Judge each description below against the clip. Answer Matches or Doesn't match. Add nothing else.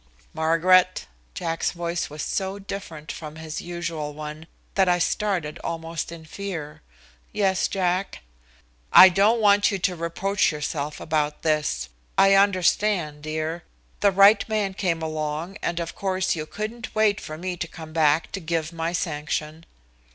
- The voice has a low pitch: Doesn't match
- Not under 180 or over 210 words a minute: Doesn't match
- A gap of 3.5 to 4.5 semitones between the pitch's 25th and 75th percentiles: Matches